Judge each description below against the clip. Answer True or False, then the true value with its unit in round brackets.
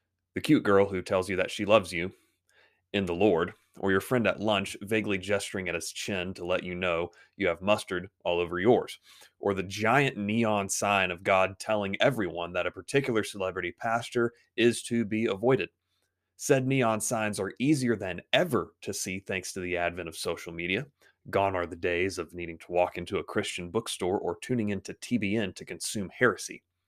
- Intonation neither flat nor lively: True (3.4 semitones)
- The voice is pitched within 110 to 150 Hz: False (100 Hz)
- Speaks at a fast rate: False (190 wpm)